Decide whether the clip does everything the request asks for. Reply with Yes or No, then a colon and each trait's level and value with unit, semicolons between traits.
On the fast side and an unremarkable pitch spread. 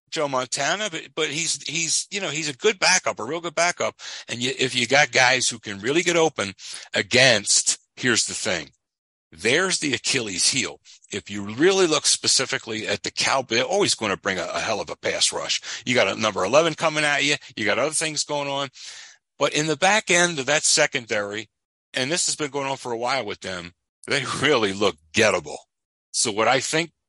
Yes: fast, 215 wpm; average, 4.4 semitones